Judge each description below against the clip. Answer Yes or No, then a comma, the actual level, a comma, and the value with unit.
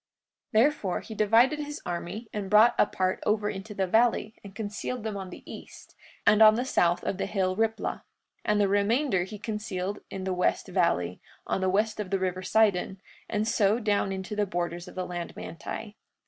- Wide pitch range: No, average, 2.8 semitones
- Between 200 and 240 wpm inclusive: Yes, fast, 205 wpm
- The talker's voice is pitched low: No, high, 205 Hz